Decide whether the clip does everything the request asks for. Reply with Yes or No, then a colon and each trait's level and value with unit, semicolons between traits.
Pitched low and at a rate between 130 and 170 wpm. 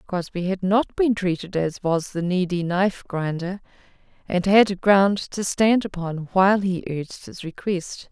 No: medium, 185 Hz; average, 165 wpm